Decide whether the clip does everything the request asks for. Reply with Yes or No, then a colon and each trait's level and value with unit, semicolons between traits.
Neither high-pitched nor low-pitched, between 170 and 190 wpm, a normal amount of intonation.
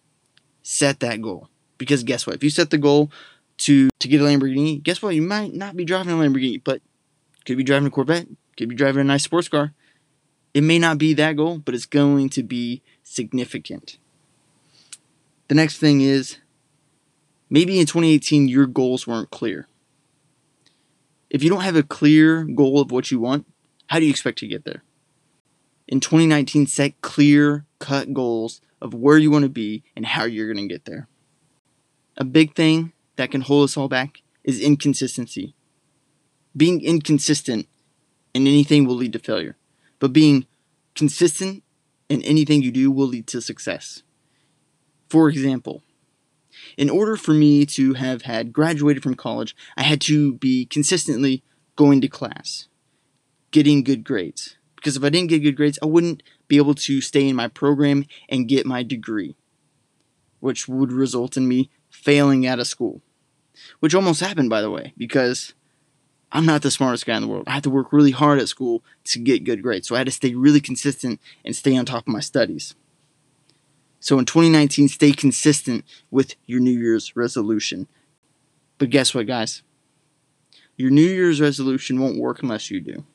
No: medium, 145 Hz; average, 175 wpm; narrow, 2.2 semitones